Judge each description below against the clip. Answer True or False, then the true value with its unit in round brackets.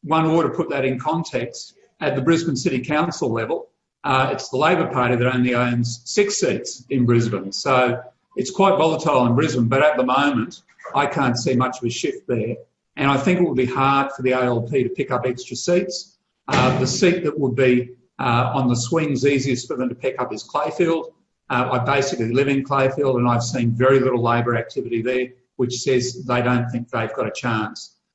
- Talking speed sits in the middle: False (210 wpm)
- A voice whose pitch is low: True (130 Hz)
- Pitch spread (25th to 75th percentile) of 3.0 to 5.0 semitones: True (3.5 semitones)